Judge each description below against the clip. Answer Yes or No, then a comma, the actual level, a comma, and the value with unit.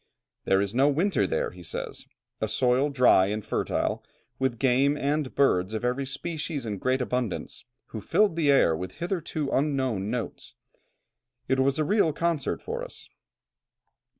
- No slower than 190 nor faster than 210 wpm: No, average, 155 wpm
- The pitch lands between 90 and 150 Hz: Yes, low, 135 Hz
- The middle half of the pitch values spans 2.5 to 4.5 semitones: No, average, 5.1 semitones